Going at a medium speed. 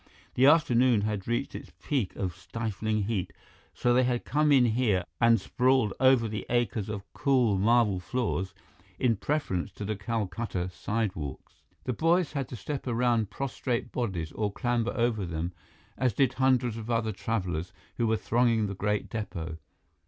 Yes: average, 160 wpm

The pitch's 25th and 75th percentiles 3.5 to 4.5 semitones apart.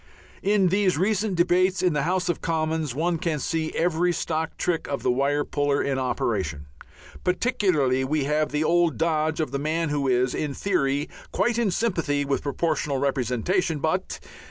Yes: average, 4.1 semitones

